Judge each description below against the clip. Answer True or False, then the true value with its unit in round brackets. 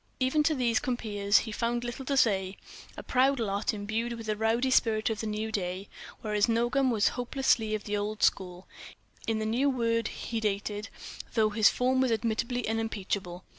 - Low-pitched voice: False (225 Hz)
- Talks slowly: False (170 wpm)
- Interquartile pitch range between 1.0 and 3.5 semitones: True (2.5 semitones)